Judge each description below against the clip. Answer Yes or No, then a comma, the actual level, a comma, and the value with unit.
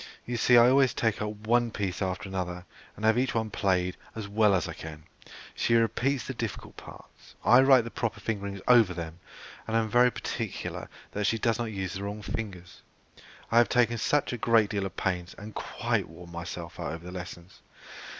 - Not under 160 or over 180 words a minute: No, average, 200 wpm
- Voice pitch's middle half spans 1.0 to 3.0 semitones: No, average, 4.0 semitones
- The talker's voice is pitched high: No, low, 105 Hz